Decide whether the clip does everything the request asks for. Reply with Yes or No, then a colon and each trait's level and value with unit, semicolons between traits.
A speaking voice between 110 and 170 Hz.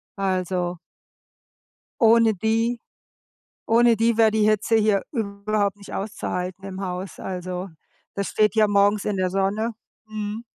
No: high, 205 Hz